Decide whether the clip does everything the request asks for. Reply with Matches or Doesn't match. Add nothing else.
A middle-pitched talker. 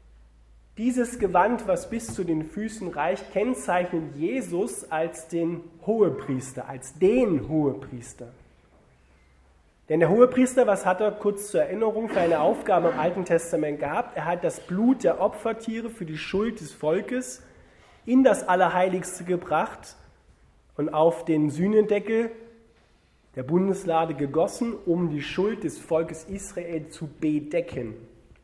Matches